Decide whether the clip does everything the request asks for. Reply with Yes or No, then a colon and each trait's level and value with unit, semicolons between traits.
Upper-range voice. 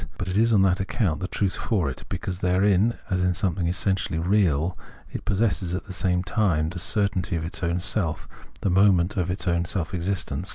No: very low, 90 Hz